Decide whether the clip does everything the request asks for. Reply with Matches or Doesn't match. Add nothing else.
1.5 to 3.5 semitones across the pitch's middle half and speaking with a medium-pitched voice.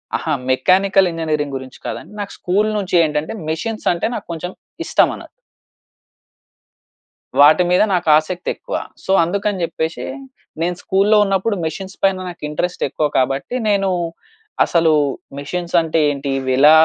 Doesn't match